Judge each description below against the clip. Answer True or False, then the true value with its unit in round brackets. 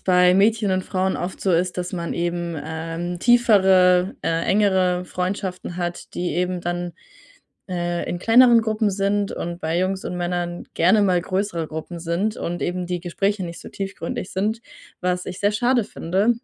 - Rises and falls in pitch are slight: True (2.3 semitones)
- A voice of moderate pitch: True (180 Hz)